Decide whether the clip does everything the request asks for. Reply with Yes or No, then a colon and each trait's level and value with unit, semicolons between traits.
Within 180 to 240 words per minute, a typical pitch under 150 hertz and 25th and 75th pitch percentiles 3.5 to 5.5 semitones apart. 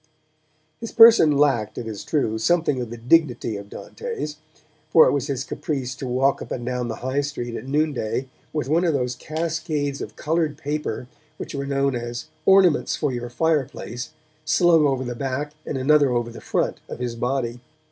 Yes: average, 185 wpm; medium, 140 Hz; average, 3.9 semitones